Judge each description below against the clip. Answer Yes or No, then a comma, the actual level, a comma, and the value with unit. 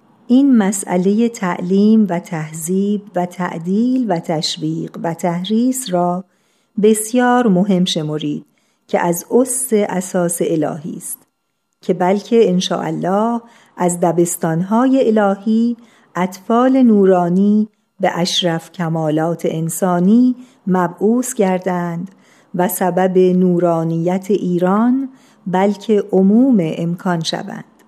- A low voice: No, high, 190 Hz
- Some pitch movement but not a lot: Yes, average, 4.0 semitones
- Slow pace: Yes, slow, 95 wpm